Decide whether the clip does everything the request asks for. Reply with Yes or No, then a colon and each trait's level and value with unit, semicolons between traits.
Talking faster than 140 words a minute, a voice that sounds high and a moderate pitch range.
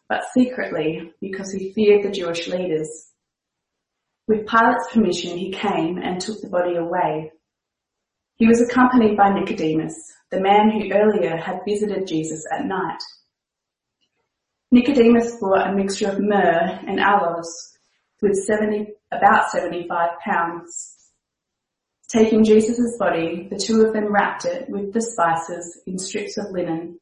No: slow, 135 wpm; high, 195 Hz; average, 4.0 semitones